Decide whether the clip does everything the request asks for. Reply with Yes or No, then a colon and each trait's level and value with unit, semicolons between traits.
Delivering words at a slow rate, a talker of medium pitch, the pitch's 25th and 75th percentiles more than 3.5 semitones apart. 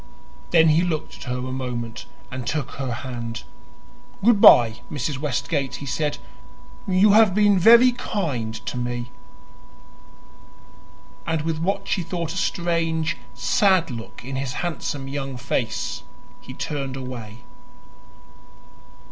Yes: slow, 125 wpm; medium, 145 Hz; wide, 5.6 semitones